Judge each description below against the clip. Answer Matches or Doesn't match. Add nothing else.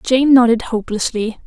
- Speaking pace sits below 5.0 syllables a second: Doesn't match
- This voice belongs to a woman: Matches